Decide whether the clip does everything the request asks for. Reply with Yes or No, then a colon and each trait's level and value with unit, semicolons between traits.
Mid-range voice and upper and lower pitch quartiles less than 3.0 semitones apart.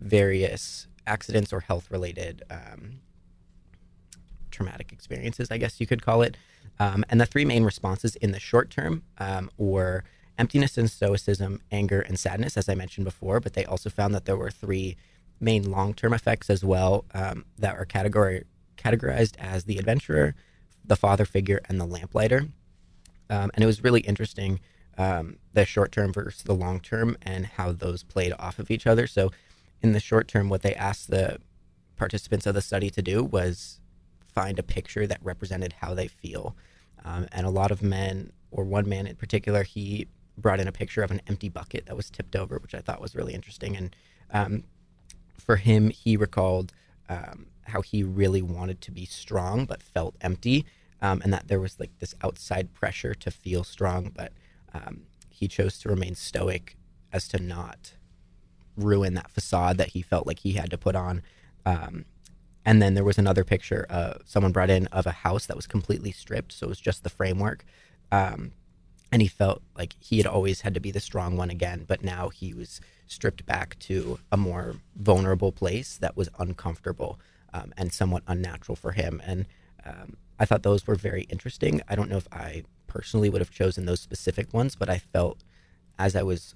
No: very low, 95 Hz; narrow, 2.4 semitones